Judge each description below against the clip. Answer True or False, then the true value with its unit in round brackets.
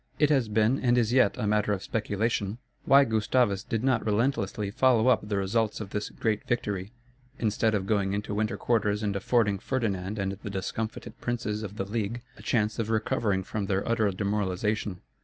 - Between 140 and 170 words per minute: False (185 wpm)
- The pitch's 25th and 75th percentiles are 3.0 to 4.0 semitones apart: False (2.4 semitones)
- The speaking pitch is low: True (105 Hz)